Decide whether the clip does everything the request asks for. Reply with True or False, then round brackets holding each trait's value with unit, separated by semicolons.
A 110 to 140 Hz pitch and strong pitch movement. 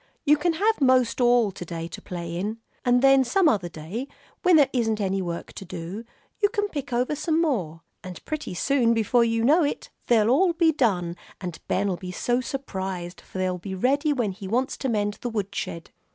False (230 Hz; 6.8 semitones)